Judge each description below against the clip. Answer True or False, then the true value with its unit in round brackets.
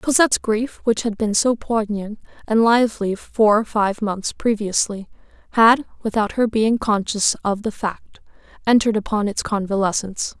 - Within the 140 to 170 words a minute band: True (150 wpm)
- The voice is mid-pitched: False (215 Hz)